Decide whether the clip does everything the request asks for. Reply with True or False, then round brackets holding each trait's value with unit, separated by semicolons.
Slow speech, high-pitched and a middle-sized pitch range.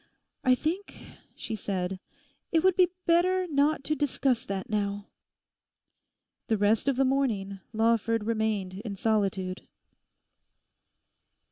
False (115 wpm; 225 Hz; 5.8 semitones)